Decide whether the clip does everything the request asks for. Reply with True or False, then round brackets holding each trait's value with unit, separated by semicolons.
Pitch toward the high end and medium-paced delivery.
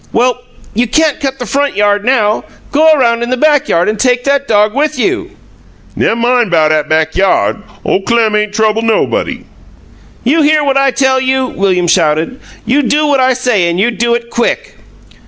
True (240 Hz; 190 wpm)